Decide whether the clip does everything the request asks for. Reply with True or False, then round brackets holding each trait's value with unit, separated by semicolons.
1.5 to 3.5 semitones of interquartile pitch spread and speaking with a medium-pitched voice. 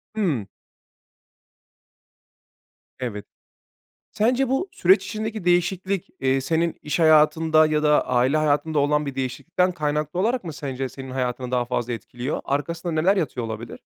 False (5.1 semitones; 150 Hz)